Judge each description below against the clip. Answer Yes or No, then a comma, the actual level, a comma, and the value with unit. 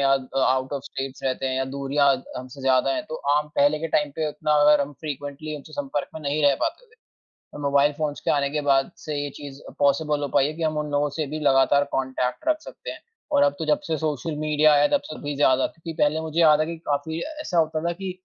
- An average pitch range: No, narrow, 2.0 semitones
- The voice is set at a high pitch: No, medium, 145 Hz